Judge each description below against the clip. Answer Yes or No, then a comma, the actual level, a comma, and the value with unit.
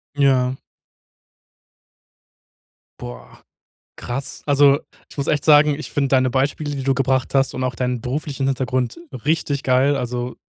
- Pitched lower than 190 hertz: Yes, low, 135 Hz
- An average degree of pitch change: No, narrow, 2.0 semitones